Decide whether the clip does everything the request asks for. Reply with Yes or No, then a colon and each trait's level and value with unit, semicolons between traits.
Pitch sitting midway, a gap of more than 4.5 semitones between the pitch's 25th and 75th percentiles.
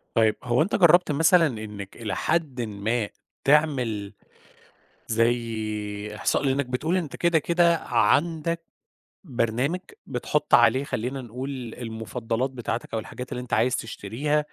No: low, 125 Hz; average, 5.1 semitones